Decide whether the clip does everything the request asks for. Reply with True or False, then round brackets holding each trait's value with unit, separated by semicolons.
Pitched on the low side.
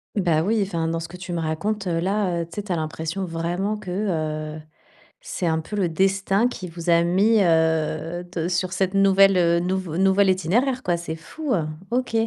False (180 Hz)